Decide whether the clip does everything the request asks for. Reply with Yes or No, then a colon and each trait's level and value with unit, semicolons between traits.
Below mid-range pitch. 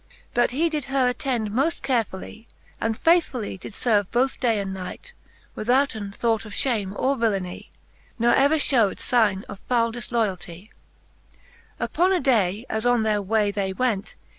No: high, 230 Hz